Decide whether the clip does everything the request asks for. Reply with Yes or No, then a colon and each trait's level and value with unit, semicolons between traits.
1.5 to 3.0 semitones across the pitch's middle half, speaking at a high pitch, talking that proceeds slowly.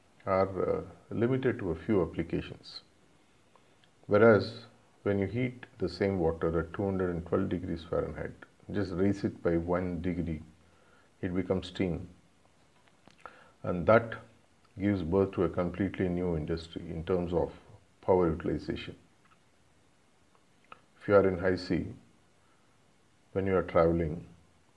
No: narrow, 2.6 semitones; very low, 95 Hz; slow, 125 wpm